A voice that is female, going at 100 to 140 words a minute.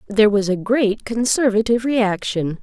Yes: female; slow, 135 wpm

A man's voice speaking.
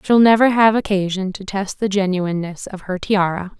No: female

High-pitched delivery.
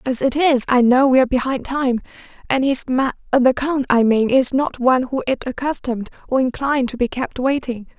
Yes: very high, 255 Hz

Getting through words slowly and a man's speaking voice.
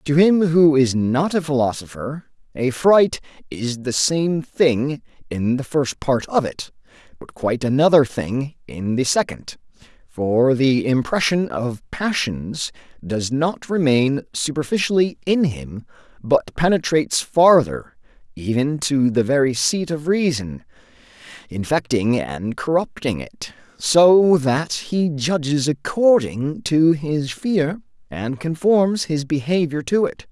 Yes: slow, 130 wpm; male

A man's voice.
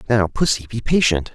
Yes: male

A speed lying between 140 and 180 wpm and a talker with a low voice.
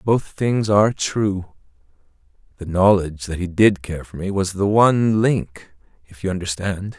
Yes: average, 165 wpm; very low, 95 Hz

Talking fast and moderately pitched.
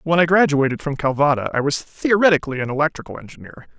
No: average, 175 wpm; medium, 150 Hz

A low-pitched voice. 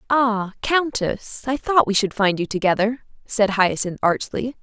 No: high, 220 Hz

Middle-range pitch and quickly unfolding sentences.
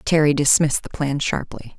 No: medium, 145 Hz; average, 170 wpm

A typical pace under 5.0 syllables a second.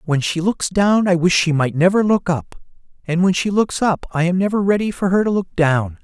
No: 5.2 syllables/s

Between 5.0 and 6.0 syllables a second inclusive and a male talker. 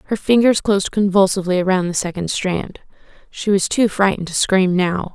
No: 5.6 syllables/s; female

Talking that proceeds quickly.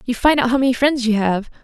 Yes: fast, 295 wpm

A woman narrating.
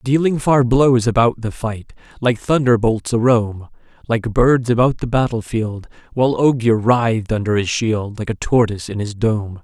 No: male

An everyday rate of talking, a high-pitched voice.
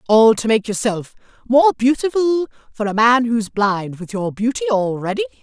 Yes: average, 165 wpm; high, 235 Hz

